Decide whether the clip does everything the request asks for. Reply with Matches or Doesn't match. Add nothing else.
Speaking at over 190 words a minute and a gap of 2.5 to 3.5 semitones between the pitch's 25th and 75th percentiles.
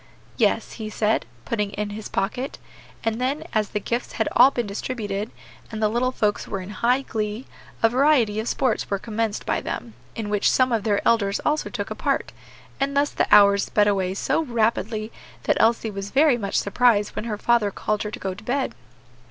Matches